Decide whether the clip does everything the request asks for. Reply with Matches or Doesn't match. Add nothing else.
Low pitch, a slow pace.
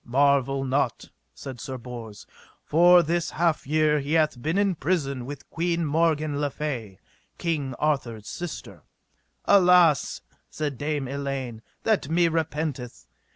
Doesn't match